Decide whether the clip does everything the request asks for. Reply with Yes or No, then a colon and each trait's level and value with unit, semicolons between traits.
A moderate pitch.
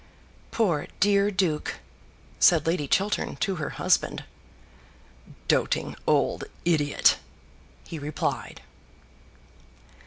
Yes: medium, 170 Hz